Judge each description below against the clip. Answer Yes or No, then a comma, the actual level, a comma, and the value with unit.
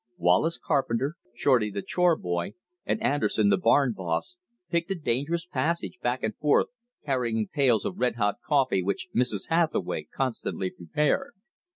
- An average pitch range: No, wide, 6.7 semitones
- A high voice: No, low, 130 Hz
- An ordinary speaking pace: Yes, average, 150 wpm